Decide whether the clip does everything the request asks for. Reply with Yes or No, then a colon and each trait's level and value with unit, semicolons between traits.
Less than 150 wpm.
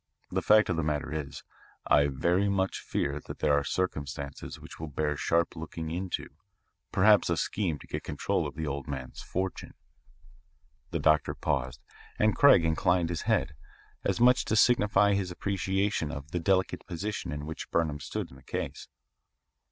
No: average, 175 wpm